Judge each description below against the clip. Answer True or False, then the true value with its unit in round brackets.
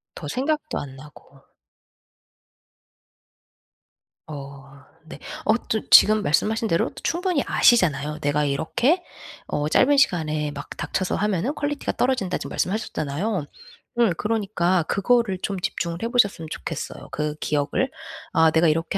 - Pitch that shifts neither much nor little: False (7.0 semitones)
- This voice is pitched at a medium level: True (180 Hz)